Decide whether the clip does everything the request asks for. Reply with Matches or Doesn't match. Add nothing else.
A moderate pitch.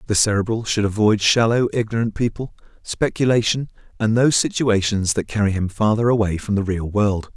Doesn't match